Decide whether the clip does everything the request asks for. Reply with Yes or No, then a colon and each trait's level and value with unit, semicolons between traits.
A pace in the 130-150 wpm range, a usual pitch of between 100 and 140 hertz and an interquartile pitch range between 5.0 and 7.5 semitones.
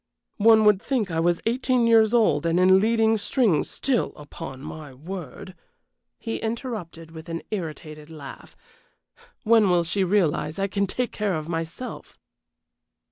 No: average, 145 wpm; high, 190 Hz; wide, 5.4 semitones